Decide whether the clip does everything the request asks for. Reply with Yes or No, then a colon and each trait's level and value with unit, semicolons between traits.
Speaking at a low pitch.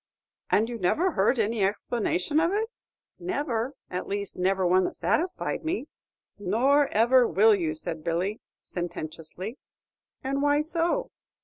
No: high, 225 Hz